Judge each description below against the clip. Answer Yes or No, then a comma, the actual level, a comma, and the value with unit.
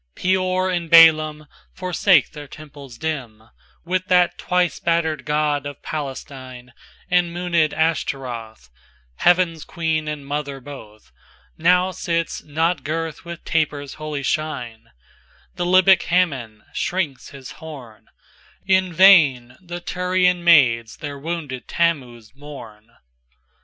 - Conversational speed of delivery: No, slow, 95 wpm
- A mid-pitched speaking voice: Yes, medium, 155 Hz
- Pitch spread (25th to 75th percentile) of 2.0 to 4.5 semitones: No, average, 4.9 semitones